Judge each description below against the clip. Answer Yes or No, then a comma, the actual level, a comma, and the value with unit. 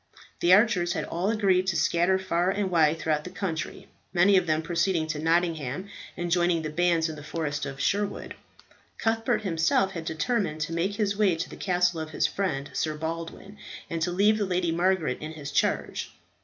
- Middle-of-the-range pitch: Yes, medium, 175 Hz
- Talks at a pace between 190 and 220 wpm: Yes, average, 195 wpm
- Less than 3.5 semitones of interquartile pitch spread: Yes, average, 3.0 semitones